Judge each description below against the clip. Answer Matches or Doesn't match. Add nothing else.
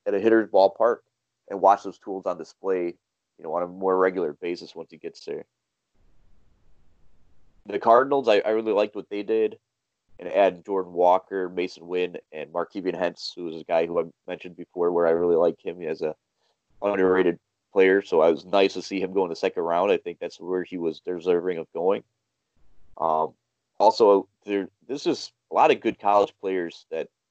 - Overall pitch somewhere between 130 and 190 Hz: Doesn't match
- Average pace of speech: Matches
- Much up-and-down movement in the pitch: Doesn't match